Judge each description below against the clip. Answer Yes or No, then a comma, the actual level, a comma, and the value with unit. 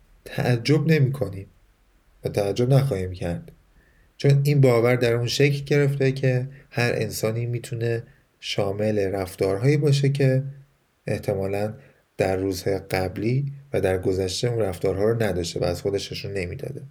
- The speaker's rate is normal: Yes, average, 130 wpm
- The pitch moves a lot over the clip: Yes, wide, 5.9 semitones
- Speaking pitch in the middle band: No, low, 120 Hz